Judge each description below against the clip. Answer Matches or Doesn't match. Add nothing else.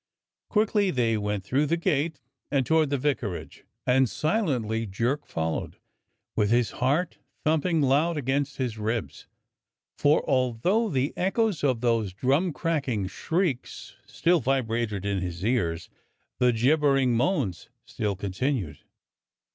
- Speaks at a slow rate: Matches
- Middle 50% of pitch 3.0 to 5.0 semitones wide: Doesn't match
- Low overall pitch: Matches